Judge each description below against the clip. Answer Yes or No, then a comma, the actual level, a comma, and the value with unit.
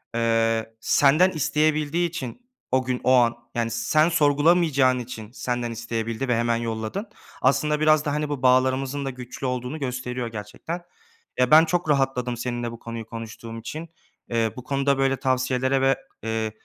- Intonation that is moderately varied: Yes, average, 3.8 semitones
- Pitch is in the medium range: No, low, 130 Hz